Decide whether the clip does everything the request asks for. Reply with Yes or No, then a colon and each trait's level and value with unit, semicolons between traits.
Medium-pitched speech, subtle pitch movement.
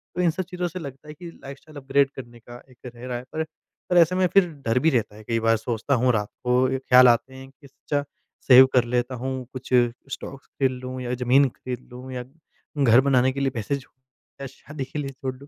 No: low, 130 Hz; narrow, 2.1 semitones